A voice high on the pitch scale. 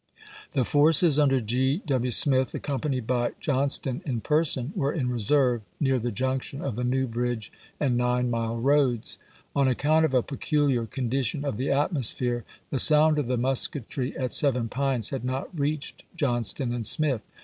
No: low, 130 Hz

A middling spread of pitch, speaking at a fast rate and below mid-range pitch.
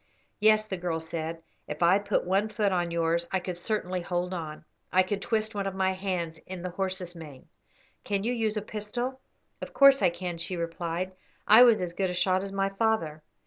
No: average, 3.4 semitones; fast, 210 wpm; medium, 185 Hz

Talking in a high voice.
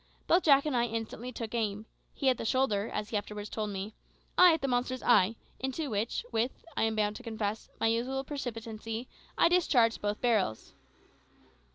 Yes: high, 230 Hz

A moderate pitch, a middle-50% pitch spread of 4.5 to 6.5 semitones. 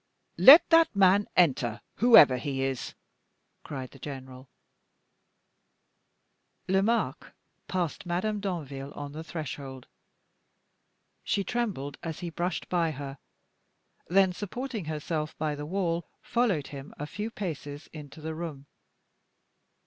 Yes: medium, 160 Hz; average, 5.2 semitones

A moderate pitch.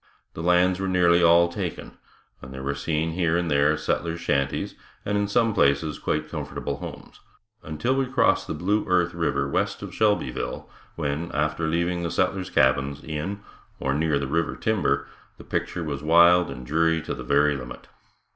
No: very low, 85 Hz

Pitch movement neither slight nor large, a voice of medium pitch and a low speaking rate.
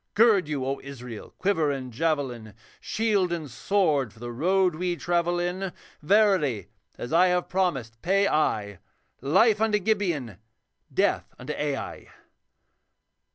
No: wide, 6.5 semitones; medium, 165 Hz; slow, 130 wpm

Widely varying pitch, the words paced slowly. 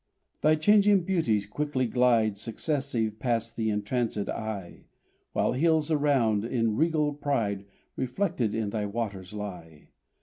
Yes: wide, 5.9 semitones; slow, 125 wpm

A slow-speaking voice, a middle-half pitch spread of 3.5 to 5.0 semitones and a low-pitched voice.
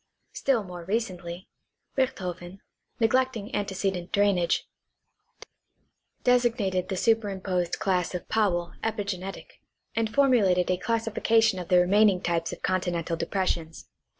No: slow, 110 wpm; average, 3.8 semitones; high, 190 Hz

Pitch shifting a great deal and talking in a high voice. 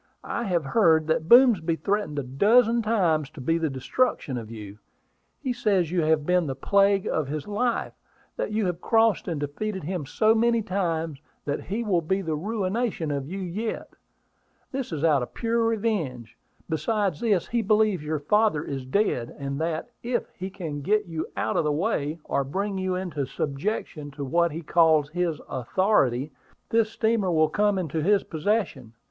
No: wide, 6.0 semitones; medium, 175 Hz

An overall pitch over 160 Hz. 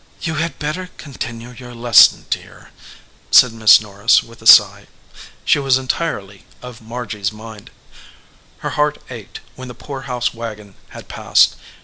No: low, 120 Hz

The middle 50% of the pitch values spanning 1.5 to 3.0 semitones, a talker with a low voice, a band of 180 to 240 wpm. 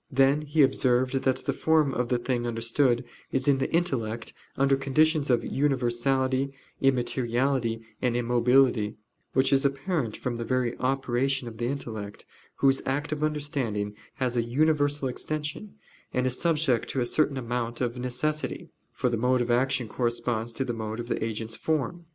No: average, 2.7 semitones; low, 130 Hz; average, 165 wpm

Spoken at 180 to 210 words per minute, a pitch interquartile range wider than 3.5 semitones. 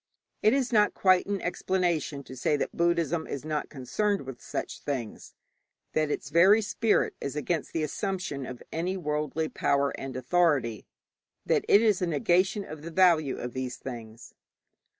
No: average, 165 wpm; average, 5.2 semitones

